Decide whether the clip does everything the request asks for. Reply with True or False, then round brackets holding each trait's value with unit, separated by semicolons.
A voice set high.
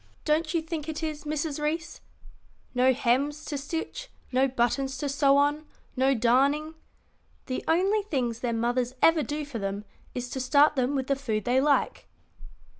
True (280 Hz)